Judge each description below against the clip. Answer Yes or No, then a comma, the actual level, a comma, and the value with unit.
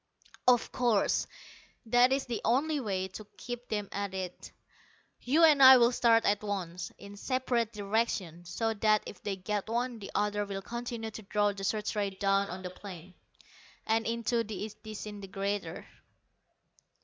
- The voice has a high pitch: Yes, high, 210 Hz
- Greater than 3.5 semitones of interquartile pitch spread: No, average, 3.1 semitones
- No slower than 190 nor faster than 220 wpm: No, average, 160 wpm